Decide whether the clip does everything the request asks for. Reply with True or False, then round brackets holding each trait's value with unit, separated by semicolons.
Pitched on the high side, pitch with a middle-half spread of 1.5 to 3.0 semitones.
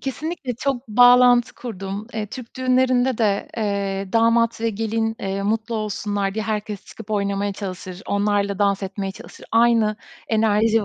True (215 Hz; 2.5 semitones)